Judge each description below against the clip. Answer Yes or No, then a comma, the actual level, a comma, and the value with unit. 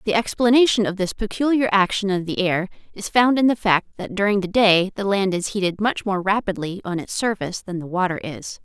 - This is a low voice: No, high, 200 Hz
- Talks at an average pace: No, fast, 220 wpm